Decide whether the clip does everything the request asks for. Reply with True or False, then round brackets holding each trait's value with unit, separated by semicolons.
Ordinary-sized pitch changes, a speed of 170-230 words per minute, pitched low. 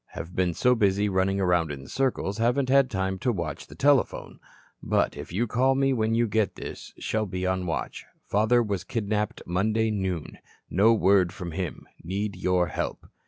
True (3.7 semitones; 185 wpm; 100 Hz)